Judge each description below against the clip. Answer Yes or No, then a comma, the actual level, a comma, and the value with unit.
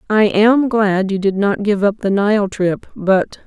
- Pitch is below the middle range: No, high, 205 Hz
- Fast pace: Yes, fast, 210 wpm